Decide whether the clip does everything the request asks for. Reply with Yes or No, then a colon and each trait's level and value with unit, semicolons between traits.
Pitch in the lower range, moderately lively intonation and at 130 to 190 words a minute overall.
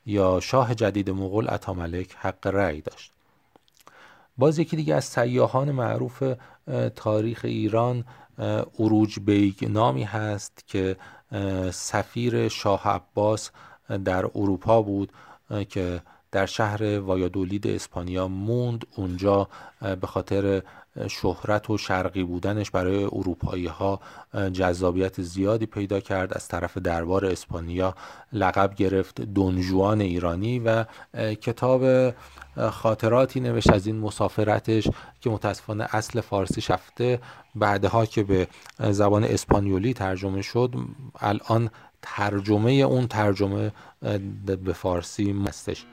No: low, 100 Hz; average, 3.0 semitones; slow, 105 wpm